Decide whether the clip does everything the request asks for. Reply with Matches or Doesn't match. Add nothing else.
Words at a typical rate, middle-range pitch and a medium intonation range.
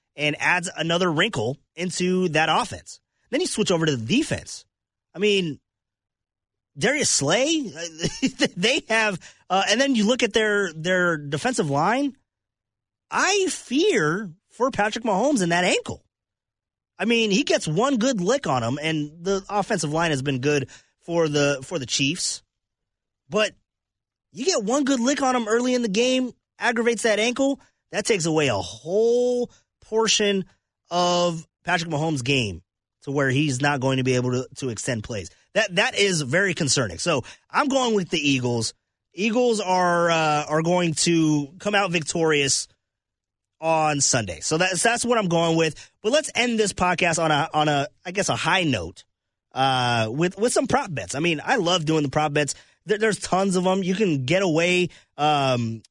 Doesn't match